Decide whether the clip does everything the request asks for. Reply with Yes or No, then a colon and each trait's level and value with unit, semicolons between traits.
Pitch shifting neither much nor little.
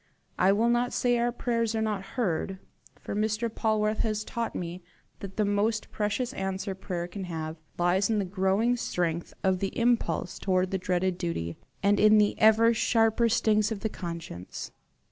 Yes: average, 3.3 semitones